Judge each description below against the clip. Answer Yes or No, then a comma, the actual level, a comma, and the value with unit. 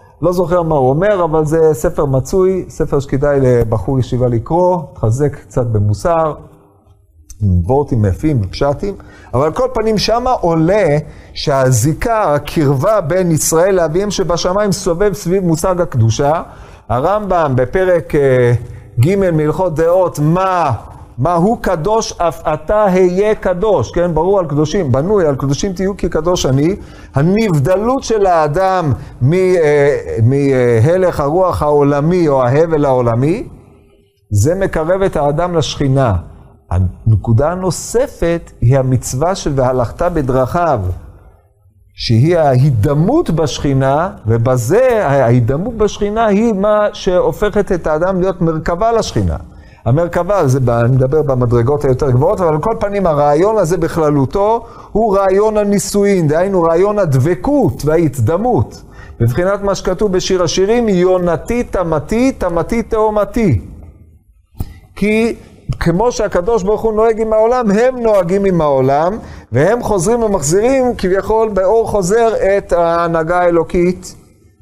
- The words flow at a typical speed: Yes, average, 115 wpm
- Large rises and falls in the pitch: Yes, wide, 6.9 semitones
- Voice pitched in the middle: Yes, medium, 165 Hz